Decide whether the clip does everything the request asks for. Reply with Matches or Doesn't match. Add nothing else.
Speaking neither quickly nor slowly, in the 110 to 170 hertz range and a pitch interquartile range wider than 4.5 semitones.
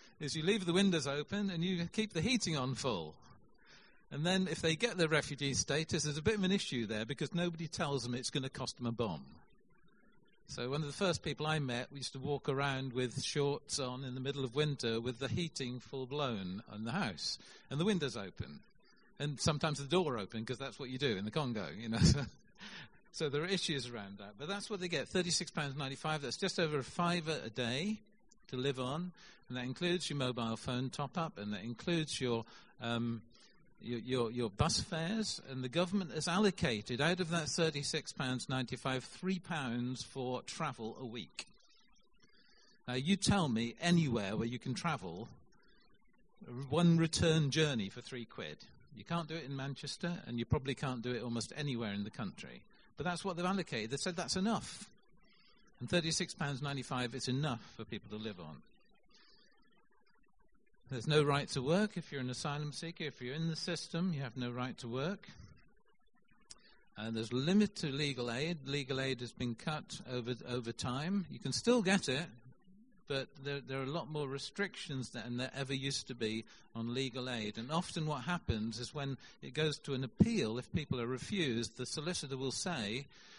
Matches